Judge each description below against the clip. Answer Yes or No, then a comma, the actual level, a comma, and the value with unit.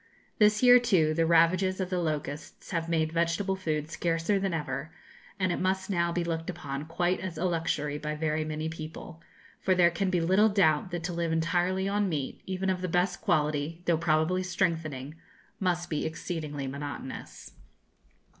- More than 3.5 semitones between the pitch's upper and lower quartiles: No, average, 2.9 semitones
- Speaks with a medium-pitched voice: Yes, medium, 170 Hz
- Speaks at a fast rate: No, average, 175 wpm